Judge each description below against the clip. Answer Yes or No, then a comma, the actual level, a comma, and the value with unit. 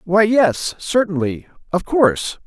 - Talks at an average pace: No, slow, 120 wpm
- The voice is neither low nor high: Yes, medium, 180 Hz